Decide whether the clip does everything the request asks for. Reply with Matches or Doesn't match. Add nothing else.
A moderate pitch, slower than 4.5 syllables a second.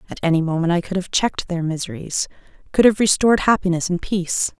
Doesn't match